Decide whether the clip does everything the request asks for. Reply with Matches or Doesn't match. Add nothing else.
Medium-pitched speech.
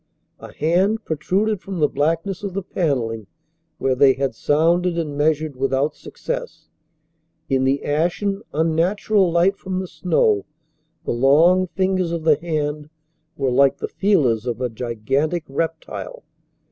Matches